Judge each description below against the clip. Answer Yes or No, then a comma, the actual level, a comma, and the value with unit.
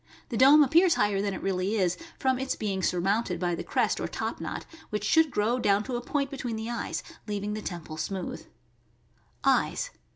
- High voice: Yes, high, 210 Hz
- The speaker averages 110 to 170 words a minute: No, average, 200 wpm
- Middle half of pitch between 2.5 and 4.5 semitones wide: No, average, 5.1 semitones